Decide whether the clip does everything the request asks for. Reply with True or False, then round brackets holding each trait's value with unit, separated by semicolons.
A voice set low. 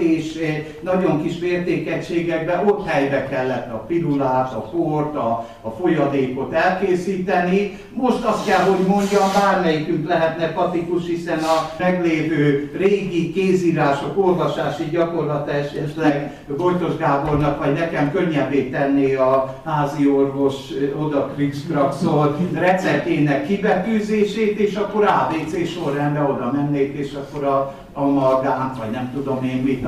False (155 Hz)